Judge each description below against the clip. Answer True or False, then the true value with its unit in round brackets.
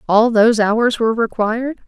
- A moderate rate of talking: True (160 wpm)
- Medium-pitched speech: False (225 Hz)